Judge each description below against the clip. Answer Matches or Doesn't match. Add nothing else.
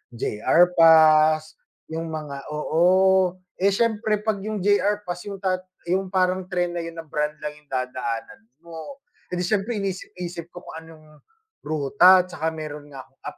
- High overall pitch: Doesn't match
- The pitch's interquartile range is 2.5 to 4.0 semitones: Matches